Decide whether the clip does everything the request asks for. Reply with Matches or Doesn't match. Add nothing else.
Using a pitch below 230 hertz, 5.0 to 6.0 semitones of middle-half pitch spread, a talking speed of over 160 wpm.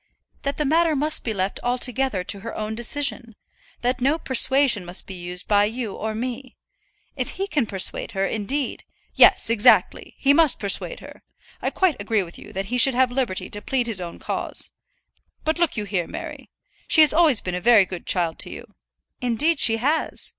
Doesn't match